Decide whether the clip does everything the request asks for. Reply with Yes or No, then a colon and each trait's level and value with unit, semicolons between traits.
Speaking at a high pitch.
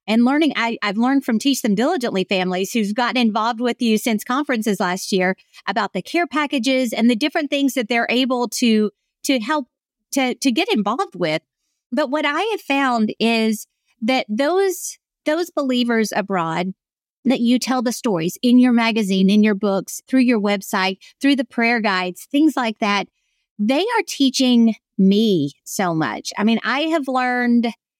Yes: high, 240 Hz